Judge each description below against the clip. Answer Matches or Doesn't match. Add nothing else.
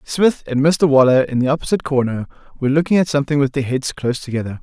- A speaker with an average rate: Doesn't match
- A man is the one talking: Matches